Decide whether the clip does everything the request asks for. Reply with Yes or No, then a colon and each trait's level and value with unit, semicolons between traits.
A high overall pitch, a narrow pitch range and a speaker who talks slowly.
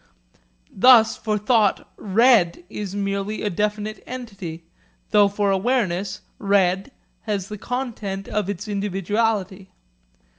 Yes: high, 205 Hz; narrow, 2.0 semitones; slow, 110 wpm